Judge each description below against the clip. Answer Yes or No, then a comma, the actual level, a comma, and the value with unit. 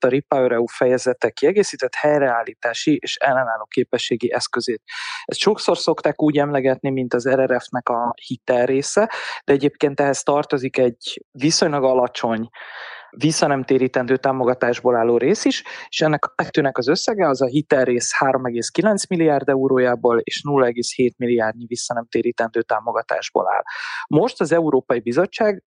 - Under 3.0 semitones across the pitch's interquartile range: No, average, 3.8 semitones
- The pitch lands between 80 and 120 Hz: No, low, 135 Hz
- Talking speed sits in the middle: Yes, average, 125 wpm